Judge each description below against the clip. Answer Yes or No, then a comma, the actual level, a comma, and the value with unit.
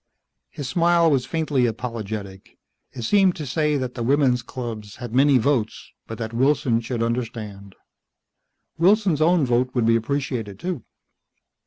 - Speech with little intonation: No, average, 4.3 semitones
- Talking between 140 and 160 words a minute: Yes, average, 145 wpm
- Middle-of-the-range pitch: No, low, 125 Hz